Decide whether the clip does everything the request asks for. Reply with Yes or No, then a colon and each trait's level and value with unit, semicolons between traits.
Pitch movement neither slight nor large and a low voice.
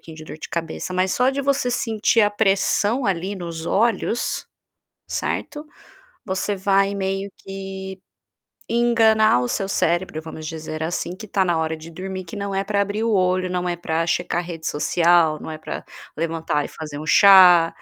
No: average, 3.6 semitones; medium, 185 Hz